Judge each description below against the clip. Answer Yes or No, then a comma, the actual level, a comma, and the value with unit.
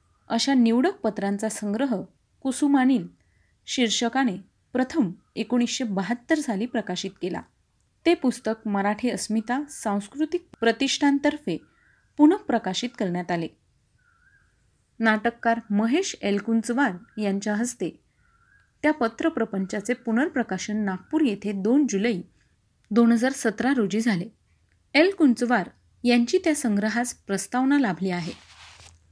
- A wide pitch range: No, average, 4.6 semitones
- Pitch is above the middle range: Yes, high, 235 Hz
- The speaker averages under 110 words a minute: Yes, average, 95 wpm